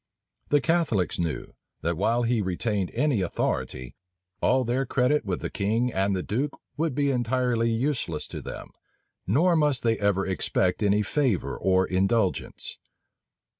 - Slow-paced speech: No, average, 145 wpm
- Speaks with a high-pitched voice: No, low, 115 Hz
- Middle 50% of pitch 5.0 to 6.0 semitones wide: Yes, wide, 5.4 semitones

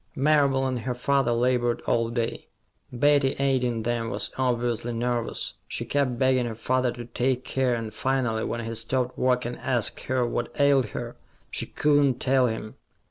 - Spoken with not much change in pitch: Yes, narrow, 2.0 semitones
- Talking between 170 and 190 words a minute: Yes, average, 175 wpm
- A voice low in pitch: Yes, low, 125 Hz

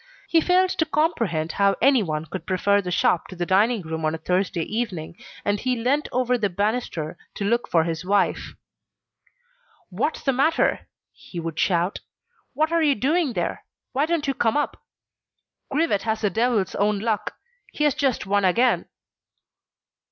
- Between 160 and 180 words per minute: Yes, average, 165 wpm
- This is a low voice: No, high, 210 Hz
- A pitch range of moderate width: No, wide, 7.0 semitones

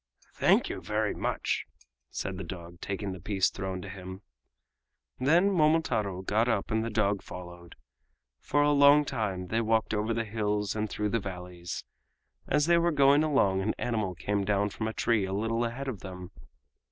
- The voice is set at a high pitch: No, low, 105 Hz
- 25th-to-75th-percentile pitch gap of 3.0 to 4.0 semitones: Yes, average, 3.5 semitones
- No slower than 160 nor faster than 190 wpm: Yes, average, 180 wpm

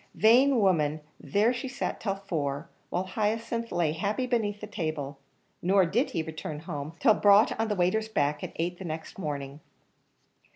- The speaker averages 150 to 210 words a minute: Yes, average, 170 wpm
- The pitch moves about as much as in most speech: No, wide, 5.7 semitones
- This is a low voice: No, high, 190 Hz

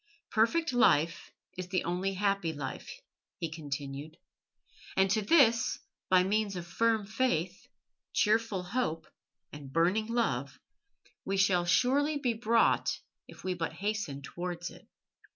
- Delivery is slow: Yes, slow, 130 wpm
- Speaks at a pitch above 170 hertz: Yes, high, 190 Hz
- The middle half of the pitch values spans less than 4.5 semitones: No, average, 4.9 semitones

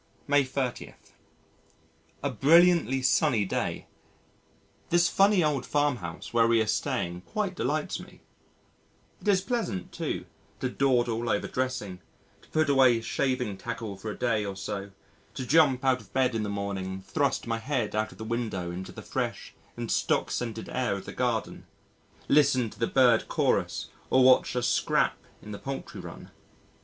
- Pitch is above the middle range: No, low, 125 Hz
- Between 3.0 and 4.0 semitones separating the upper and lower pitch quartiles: No, average, 4.5 semitones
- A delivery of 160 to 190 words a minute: Yes, average, 170 wpm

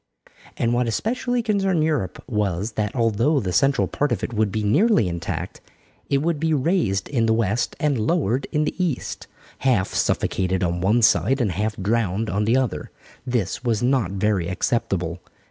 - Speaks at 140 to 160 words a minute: No, average, 175 wpm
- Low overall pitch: Yes, low, 115 Hz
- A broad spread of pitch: Yes, wide, 5.9 semitones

